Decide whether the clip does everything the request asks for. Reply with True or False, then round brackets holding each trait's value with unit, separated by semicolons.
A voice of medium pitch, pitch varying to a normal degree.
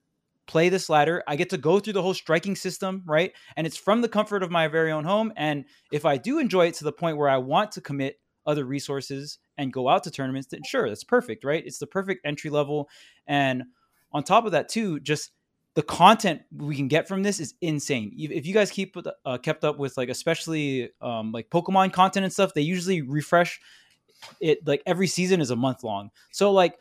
True (160 Hz; 4.8 semitones)